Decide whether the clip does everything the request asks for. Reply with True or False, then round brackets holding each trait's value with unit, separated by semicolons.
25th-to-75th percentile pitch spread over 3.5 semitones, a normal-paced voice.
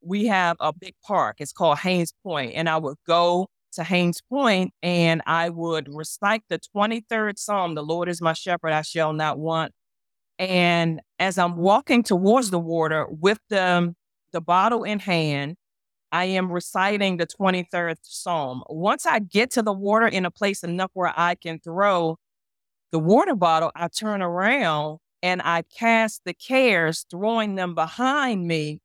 True (3.9 semitones; 165 wpm)